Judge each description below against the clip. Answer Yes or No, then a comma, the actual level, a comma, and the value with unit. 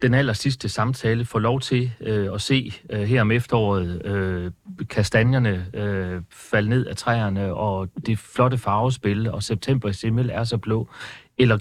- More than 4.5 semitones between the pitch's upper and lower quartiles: No, average, 3.4 semitones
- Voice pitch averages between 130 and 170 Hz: No, low, 110 Hz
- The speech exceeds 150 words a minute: Yes, average, 170 wpm